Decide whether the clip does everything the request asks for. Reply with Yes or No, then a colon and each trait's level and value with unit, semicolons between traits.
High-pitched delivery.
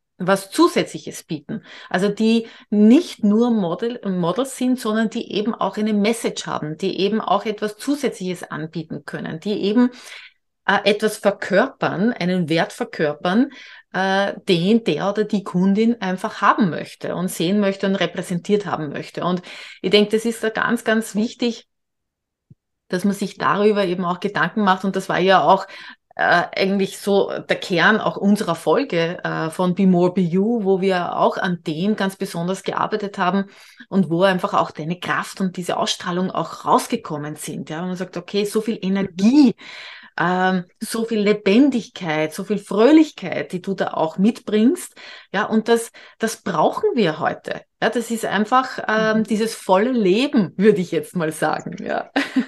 Yes: high, 200 Hz